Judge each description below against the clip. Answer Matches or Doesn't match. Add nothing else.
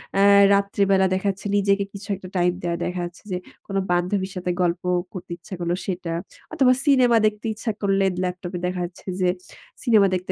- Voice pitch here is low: Doesn't match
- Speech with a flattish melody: Matches